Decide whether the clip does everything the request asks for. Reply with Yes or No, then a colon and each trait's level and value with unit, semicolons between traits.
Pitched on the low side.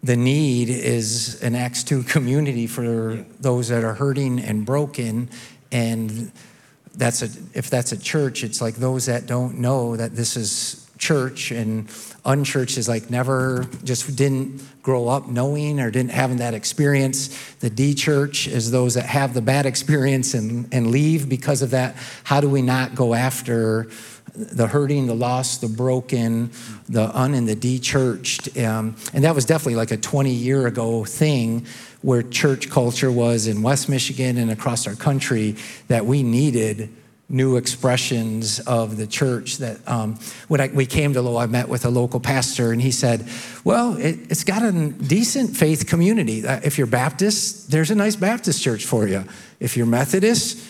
Yes: low, 125 Hz